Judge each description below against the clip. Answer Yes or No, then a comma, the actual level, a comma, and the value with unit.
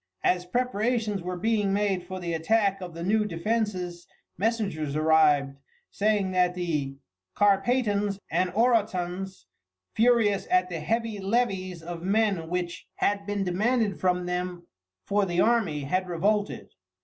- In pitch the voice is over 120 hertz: Yes, high, 190 Hz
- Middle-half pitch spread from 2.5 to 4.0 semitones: Yes, average, 3.2 semitones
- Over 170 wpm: No, slow, 135 wpm